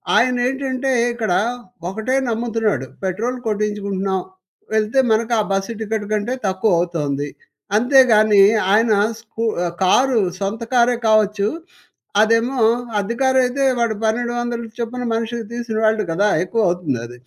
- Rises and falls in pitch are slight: No, average, 3.0 semitones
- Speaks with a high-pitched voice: Yes, high, 220 Hz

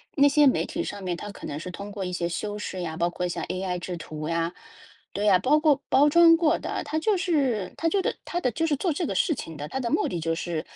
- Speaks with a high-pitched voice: Yes, high, 205 Hz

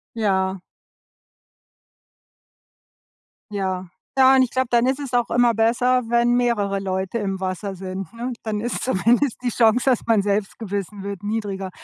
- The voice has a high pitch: Yes, high, 220 Hz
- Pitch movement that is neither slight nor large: Yes, average, 3.7 semitones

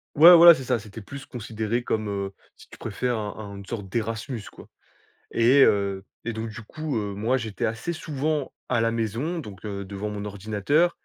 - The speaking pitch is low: Yes, low, 115 Hz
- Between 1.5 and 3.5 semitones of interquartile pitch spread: No, average, 4.3 semitones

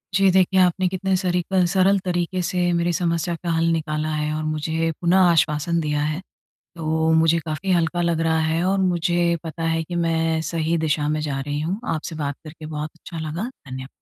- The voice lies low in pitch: No, medium, 165 Hz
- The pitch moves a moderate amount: No, narrow, 2.1 semitones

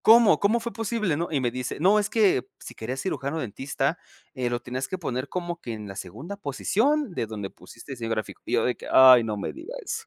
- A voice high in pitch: No, medium, 140 Hz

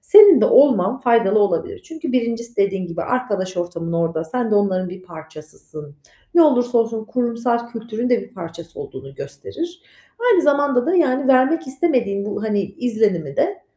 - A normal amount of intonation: No, wide, 5.9 semitones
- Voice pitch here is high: Yes, high, 230 Hz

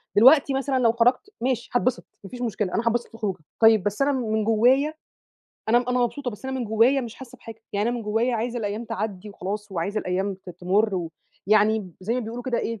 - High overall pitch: Yes, high, 225 Hz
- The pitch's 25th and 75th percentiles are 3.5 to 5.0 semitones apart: No, average, 3.0 semitones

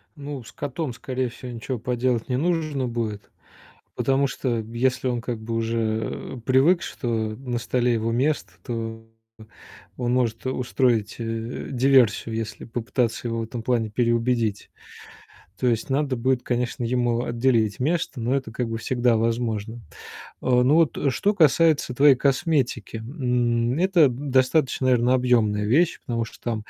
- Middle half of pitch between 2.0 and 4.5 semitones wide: Yes, narrow, 2.4 semitones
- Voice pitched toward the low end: Yes, low, 125 Hz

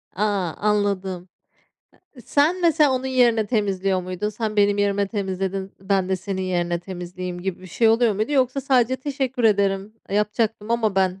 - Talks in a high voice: Yes, high, 205 Hz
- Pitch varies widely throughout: No, average, 3.7 semitones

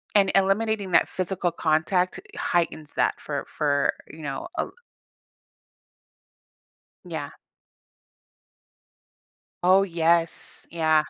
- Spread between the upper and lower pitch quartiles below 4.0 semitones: Yes, average, 3.3 semitones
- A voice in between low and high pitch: Yes, medium, 170 Hz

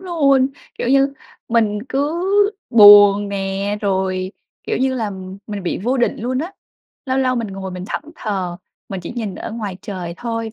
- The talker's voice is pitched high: Yes, high, 210 Hz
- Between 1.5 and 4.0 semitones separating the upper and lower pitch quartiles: No, average, 4.9 semitones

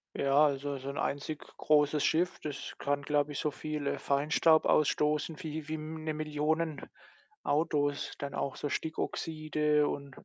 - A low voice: No, medium, 150 Hz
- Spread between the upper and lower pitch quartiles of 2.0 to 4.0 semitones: No, narrow, 1.5 semitones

